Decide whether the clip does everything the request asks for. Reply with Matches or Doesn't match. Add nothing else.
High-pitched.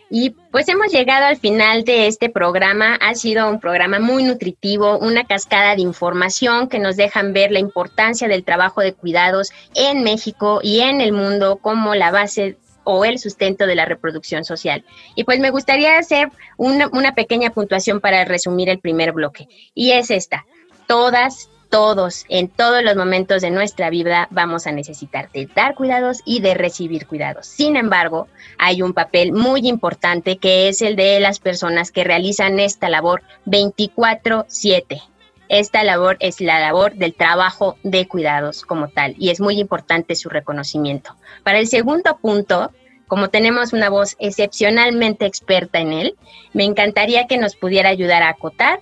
Matches